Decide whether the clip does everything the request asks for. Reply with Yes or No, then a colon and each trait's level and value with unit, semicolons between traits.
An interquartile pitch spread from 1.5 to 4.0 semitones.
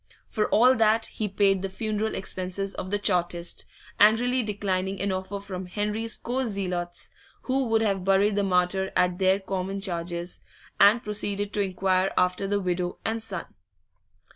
Yes: narrow, 2.4 semitones